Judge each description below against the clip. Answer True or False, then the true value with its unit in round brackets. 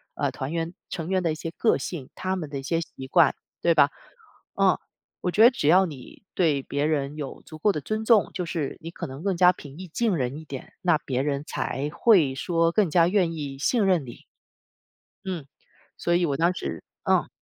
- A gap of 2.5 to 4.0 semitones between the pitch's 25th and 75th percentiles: False (4.4 semitones)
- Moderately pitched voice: True (165 Hz)